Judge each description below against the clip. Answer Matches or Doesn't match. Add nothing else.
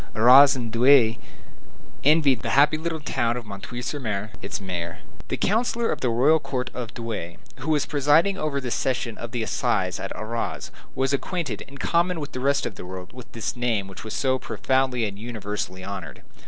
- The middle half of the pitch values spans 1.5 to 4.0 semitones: Doesn't match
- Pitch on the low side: Matches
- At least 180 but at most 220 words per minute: Matches